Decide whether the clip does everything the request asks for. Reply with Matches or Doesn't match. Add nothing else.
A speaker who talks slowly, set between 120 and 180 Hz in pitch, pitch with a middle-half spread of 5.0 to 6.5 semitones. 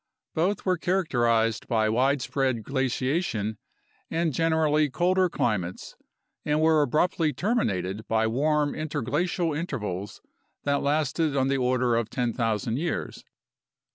Matches